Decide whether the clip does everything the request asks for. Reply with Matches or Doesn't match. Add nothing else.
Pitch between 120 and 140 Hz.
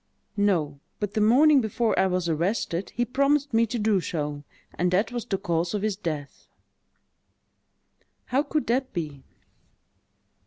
Doesn't match